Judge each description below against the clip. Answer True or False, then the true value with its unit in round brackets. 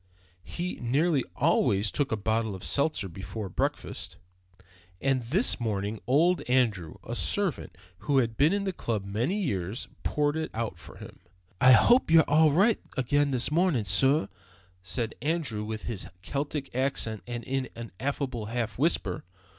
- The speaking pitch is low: True (125 Hz)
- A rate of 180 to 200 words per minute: False (155 wpm)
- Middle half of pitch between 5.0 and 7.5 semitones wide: True (5.5 semitones)